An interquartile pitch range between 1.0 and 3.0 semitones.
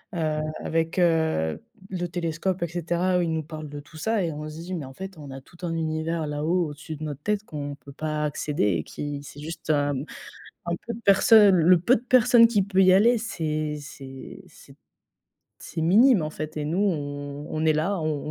No: average, 3.6 semitones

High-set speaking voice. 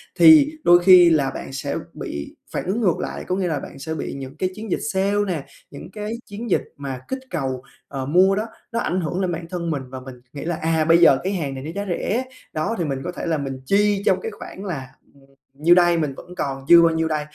No: medium, 170 Hz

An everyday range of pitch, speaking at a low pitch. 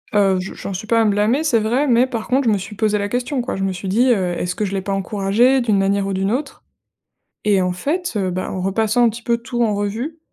No: average, 3.7 semitones; high, 210 Hz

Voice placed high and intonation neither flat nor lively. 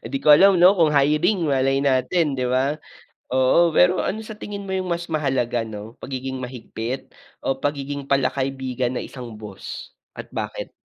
No: low, 135 Hz; average, 4.8 semitones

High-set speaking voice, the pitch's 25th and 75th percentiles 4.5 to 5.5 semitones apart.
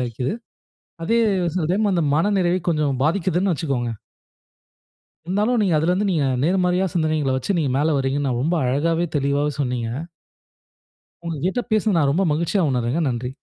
No: medium, 160 Hz; average, 5.0 semitones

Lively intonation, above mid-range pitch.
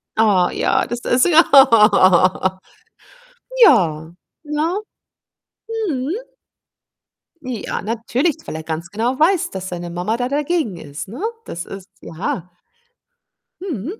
Yes: wide, 8.9 semitones; high, 225 Hz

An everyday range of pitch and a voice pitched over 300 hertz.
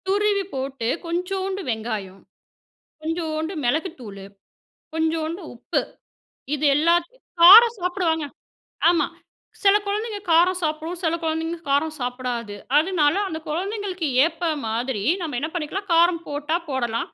Yes: average, 4.6 semitones; very high, 320 Hz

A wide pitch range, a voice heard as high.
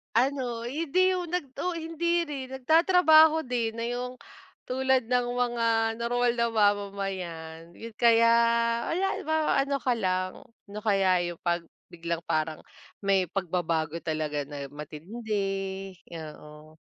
Yes: wide, 7.2 semitones; high, 225 Hz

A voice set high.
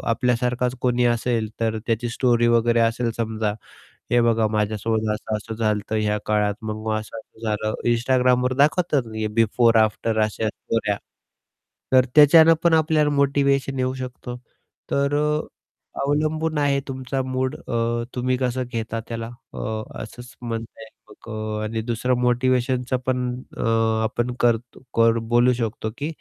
No: low, 120 Hz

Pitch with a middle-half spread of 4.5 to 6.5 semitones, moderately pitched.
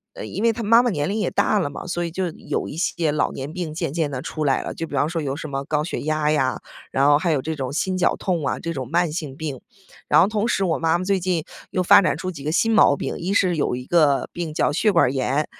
No: average, 4.0 semitones; medium, 160 Hz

